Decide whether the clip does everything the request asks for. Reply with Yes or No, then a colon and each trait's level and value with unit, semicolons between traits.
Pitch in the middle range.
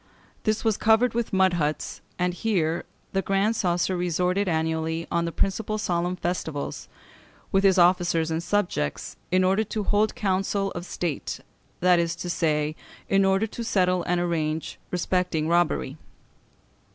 Yes: medium, 180 Hz